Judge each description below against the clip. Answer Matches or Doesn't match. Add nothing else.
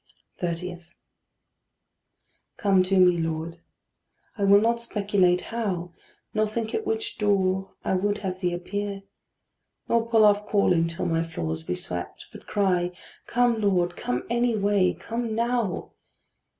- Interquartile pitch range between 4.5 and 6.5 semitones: Doesn't match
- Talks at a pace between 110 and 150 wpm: Matches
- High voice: Matches